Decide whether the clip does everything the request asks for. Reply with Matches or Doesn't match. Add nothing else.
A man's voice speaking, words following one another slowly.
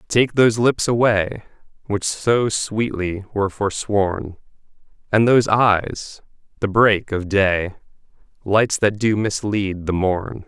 Matches